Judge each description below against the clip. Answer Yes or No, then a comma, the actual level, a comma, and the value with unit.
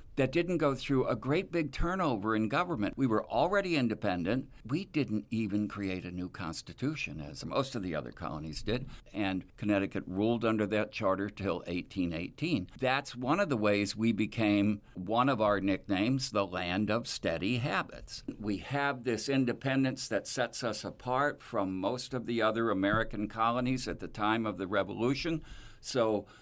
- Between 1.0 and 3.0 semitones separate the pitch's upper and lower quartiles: No, average, 4.8 semitones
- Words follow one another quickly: No, average, 170 wpm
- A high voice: No, low, 110 Hz